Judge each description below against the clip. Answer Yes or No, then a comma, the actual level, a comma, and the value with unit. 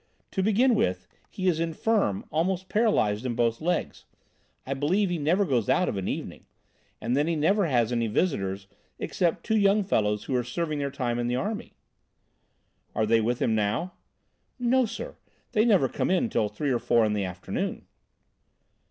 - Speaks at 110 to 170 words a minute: No, average, 180 wpm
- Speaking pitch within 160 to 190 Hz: No, medium, 145 Hz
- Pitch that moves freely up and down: Yes, wide, 8.7 semitones